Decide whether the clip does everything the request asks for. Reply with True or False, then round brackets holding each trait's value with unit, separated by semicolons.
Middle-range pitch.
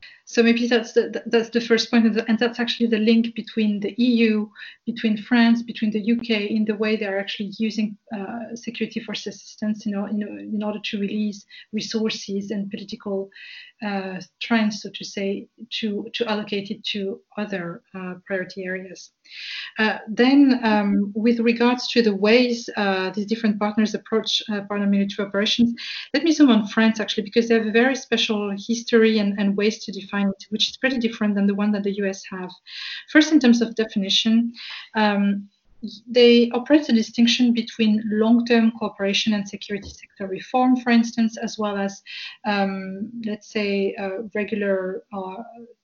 False (215 Hz)